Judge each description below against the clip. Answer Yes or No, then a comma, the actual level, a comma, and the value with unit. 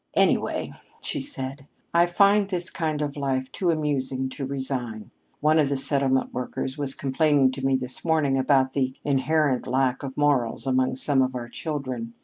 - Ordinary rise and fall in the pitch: No, narrow, 2.3 semitones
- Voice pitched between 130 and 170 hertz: Yes, low, 135 Hz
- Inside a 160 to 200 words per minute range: Yes, average, 170 wpm